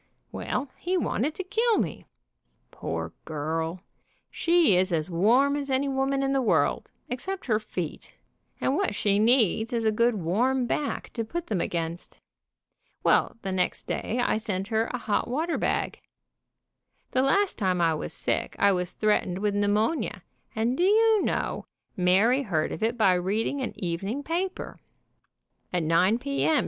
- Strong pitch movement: Yes, wide, 6.7 semitones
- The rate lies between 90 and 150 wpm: No, average, 165 wpm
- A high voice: Yes, high, 225 Hz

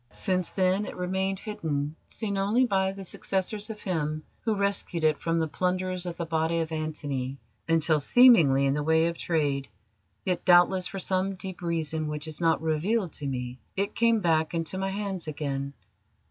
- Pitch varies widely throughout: No, average, 3.7 semitones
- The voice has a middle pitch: Yes, medium, 170 Hz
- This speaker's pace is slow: No, average, 180 wpm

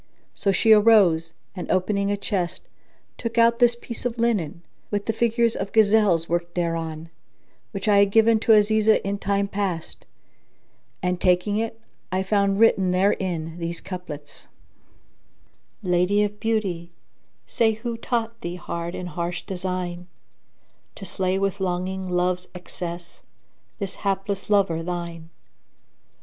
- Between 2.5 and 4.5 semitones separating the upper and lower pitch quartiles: Yes, average, 3.3 semitones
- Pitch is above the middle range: Yes, high, 195 Hz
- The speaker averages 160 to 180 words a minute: No, slow, 135 wpm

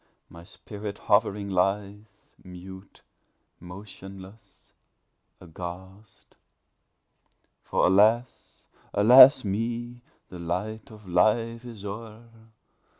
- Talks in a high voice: No, low, 100 Hz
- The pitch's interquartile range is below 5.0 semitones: Yes, average, 2.9 semitones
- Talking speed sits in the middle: No, slow, 85 wpm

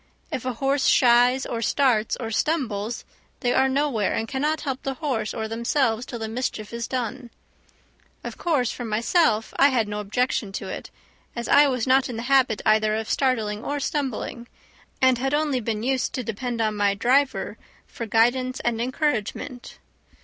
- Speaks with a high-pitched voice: Yes, high, 245 Hz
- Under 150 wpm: No, average, 175 wpm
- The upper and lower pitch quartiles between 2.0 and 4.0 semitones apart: Yes, average, 3.1 semitones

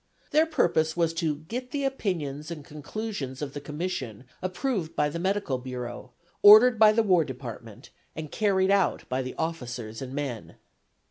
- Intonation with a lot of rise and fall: Yes, wide, 7.1 semitones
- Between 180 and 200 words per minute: No, average, 160 wpm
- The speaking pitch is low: No, medium, 160 Hz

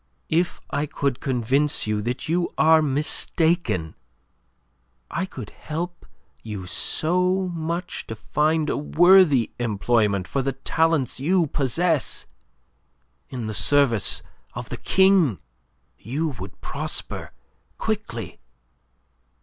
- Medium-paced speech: No, slow, 110 wpm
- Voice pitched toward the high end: No, medium, 145 Hz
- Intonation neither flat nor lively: No, wide, 6.2 semitones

